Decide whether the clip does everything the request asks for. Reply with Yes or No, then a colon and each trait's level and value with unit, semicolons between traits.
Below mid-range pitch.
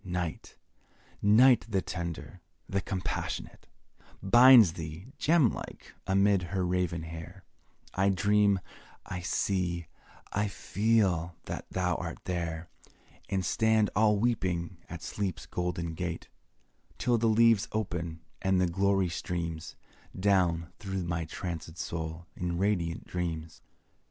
Yes: very low, 90 Hz